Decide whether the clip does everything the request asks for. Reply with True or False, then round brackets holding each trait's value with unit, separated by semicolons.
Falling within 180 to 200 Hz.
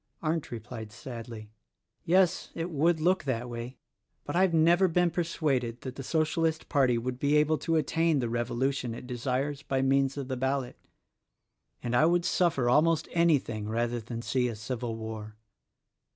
False (135 Hz)